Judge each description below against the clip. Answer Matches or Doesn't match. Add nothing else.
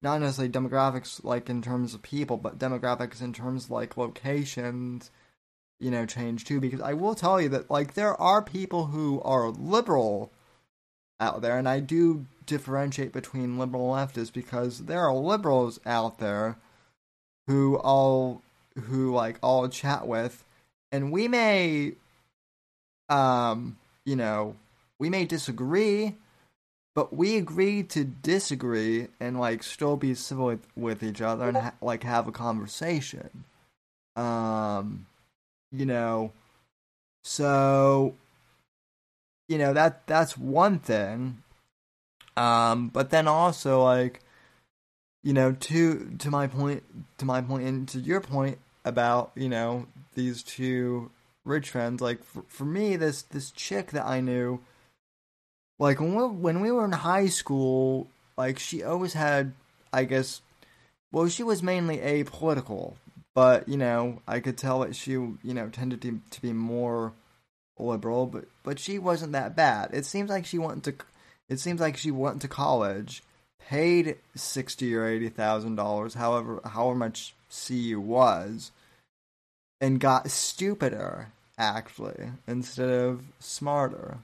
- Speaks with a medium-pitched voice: Doesn't match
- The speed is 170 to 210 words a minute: Doesn't match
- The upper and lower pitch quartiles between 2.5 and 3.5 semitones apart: Matches